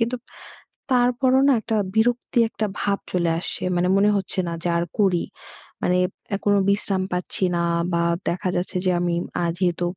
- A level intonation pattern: No, average, 4.0 semitones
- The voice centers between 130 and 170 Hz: No, high, 195 Hz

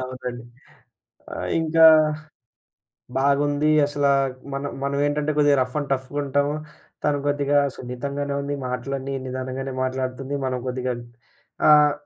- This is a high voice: No, medium, 140 Hz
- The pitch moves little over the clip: Yes, narrow, 2.0 semitones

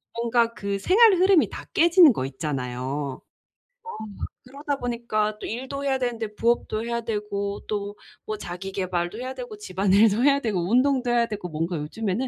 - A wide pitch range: No, average, 4.6 semitones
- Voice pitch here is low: No, high, 215 Hz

